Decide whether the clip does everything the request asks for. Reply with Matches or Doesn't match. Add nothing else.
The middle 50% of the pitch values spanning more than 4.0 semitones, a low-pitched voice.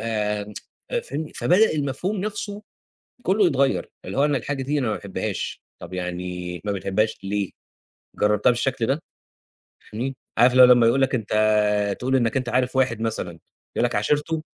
Matches